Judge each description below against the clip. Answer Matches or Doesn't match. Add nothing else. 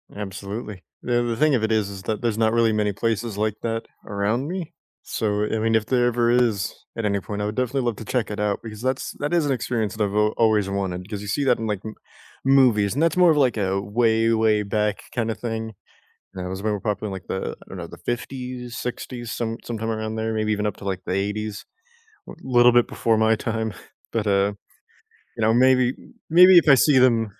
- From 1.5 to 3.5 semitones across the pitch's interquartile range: Matches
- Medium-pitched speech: Doesn't match